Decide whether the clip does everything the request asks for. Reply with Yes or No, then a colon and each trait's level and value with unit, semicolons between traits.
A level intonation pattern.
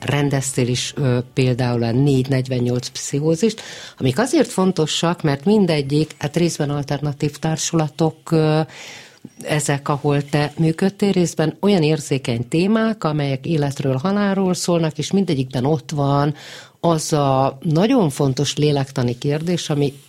No: average, 3.0 semitones